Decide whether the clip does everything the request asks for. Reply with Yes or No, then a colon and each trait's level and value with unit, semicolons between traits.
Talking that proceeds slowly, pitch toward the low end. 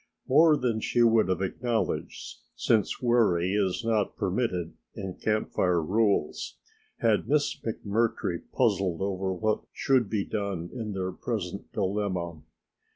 Yes: slow, 130 wpm; low, 105 Hz